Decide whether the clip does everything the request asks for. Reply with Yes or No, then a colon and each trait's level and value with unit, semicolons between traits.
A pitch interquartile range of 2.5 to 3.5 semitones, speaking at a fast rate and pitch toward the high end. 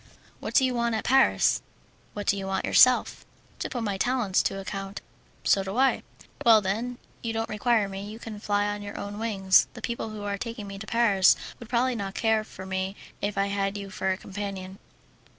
Yes: average, 2.8 semitones; fast, 210 wpm; high, 205 Hz